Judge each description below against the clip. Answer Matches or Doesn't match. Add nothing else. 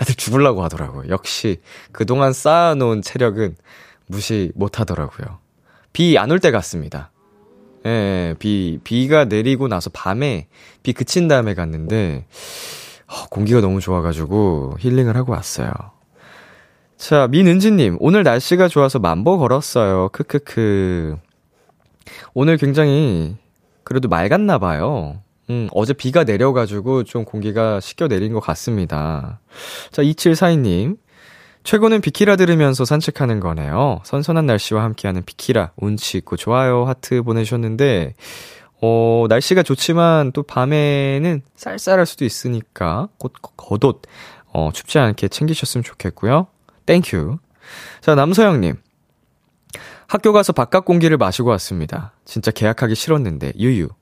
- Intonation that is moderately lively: Doesn't match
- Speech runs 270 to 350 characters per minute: Matches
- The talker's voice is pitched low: Matches